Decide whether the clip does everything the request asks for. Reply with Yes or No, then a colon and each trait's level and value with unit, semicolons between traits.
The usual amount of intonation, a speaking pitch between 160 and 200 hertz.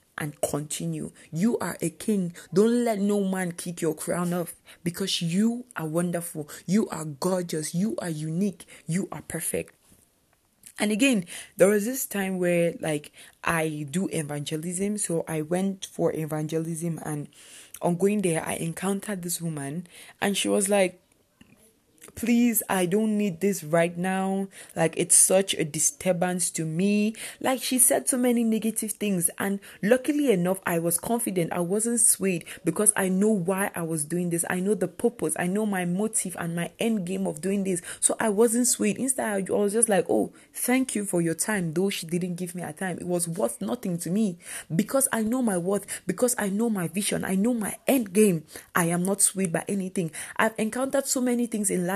Yes: average, 3.9 semitones; high, 190 Hz